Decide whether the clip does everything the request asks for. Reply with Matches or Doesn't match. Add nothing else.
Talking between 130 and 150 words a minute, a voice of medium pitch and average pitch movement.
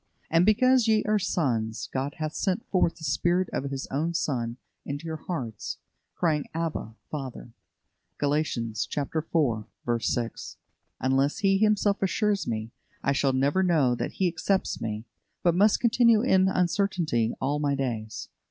Doesn't match